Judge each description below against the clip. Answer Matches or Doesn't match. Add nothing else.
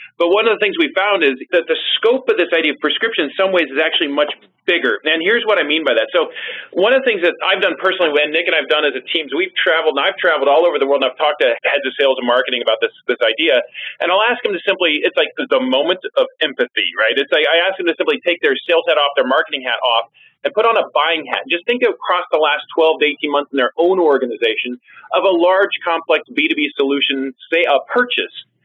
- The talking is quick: Matches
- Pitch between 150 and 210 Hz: Matches